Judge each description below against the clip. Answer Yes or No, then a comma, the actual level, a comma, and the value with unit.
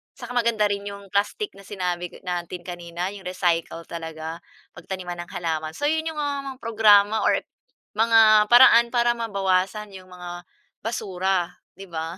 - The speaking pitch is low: No, high, 195 Hz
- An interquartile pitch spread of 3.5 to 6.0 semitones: Yes, average, 4.1 semitones